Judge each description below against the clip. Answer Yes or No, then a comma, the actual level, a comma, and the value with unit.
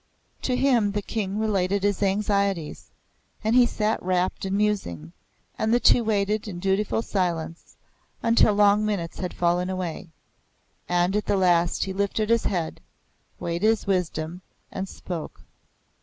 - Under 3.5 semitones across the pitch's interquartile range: Yes, average, 3.0 semitones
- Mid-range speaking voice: No, high, 195 Hz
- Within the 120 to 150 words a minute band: Yes, average, 145 wpm